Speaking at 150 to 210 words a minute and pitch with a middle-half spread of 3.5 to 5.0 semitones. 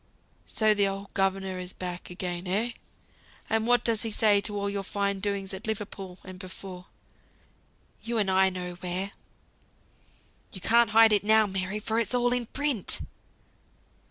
No: average, 160 wpm; narrow, 2.6 semitones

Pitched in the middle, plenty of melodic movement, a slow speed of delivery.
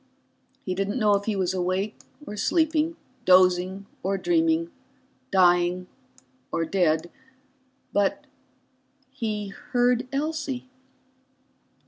No: high, 200 Hz; wide, 6.5 semitones; slow, 95 wpm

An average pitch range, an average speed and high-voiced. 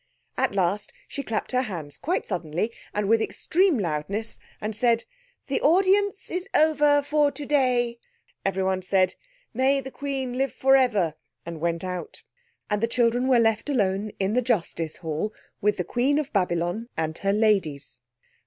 No: wide, 6.2 semitones; average, 160 wpm; high, 225 Hz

